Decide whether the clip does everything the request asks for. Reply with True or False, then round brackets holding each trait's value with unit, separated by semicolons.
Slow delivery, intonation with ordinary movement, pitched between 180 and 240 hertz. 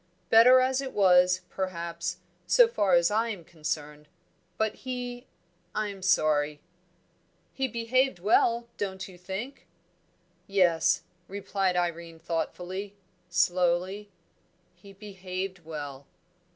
True (110 wpm; 3.8 semitones; 190 Hz)